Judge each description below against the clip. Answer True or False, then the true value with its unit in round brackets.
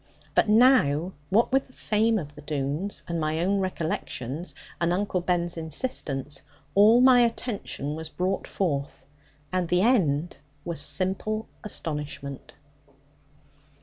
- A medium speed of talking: False (125 wpm)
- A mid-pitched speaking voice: True (175 Hz)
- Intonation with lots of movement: True (6.0 semitones)